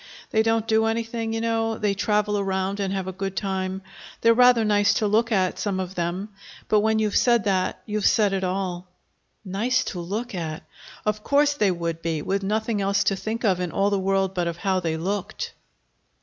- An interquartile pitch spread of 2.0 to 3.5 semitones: Yes, average, 2.8 semitones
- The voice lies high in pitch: Yes, high, 200 Hz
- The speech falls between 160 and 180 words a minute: No, fast, 205 wpm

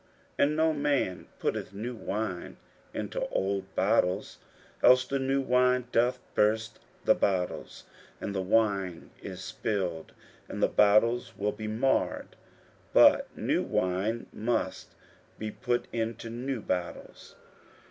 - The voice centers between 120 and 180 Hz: No, low, 110 Hz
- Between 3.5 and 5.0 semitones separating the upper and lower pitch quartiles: Yes, average, 4.3 semitones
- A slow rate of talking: Yes, slow, 125 wpm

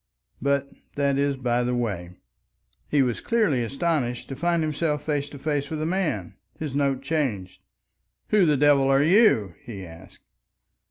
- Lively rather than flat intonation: No, average, 4.0 semitones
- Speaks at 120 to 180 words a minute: Yes, average, 160 wpm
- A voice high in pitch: No, medium, 140 Hz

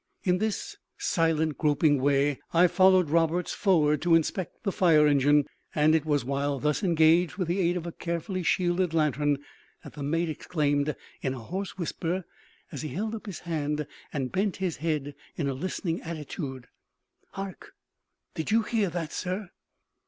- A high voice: No, medium, 165 Hz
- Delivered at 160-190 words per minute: Yes, average, 165 wpm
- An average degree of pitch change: Yes, average, 3.6 semitones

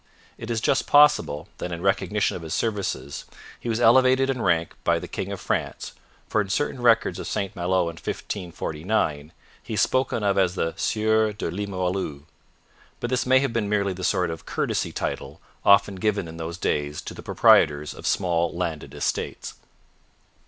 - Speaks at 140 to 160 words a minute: No, average, 180 wpm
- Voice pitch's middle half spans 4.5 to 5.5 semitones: Yes, average, 4.9 semitones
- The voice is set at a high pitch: No, very low, 95 Hz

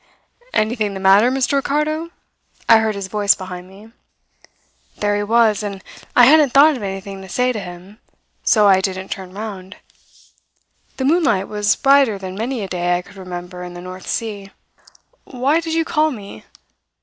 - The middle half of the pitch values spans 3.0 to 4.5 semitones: No, average, 4.9 semitones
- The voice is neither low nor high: No, high, 205 Hz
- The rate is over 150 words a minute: Yes, average, 175 wpm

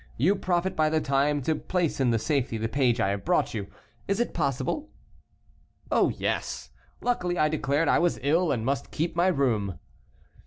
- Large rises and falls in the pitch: Yes, wide, 5.7 semitones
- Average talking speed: Yes, average, 180 wpm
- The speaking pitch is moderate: Yes, medium, 145 Hz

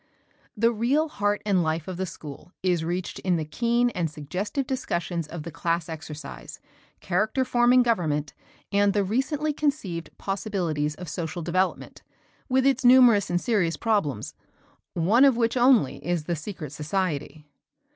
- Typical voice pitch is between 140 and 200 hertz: Yes, medium, 185 Hz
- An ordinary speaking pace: Yes, average, 150 wpm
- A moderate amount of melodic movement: No, wide, 6.5 semitones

